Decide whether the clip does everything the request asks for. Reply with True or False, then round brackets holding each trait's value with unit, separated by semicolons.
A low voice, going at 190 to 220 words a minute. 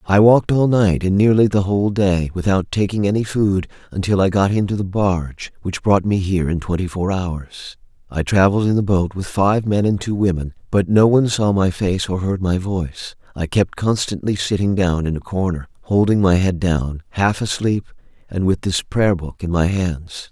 True (95 Hz; 205 wpm)